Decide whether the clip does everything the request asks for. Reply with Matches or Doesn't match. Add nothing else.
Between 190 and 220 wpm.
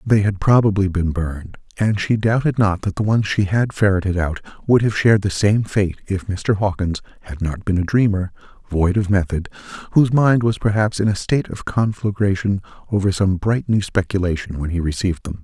Matches